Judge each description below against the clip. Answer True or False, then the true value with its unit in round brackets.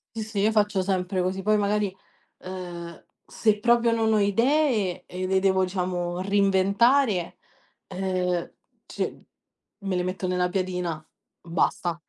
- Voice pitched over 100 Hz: True (190 Hz)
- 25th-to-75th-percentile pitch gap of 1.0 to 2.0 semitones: False (2.6 semitones)